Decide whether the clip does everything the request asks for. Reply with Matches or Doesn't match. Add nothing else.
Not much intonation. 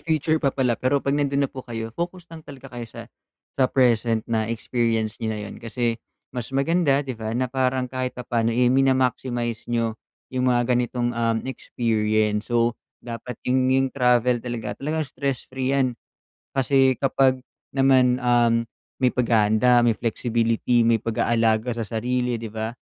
Matches